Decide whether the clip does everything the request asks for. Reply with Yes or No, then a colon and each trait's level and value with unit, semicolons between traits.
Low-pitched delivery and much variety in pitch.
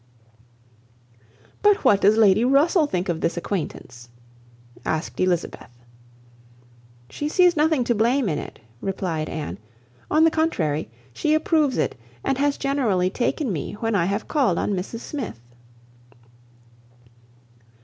No: high, 220 Hz; wide, 8.3 semitones